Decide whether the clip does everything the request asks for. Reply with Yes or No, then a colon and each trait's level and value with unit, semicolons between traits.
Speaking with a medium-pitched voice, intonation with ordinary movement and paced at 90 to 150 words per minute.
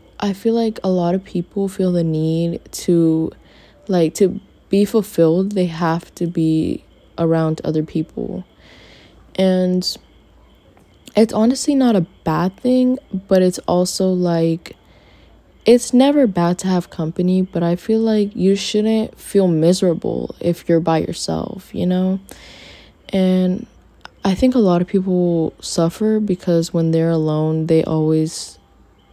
Yes: medium, 180 Hz; average, 3.3 semitones; average, 140 wpm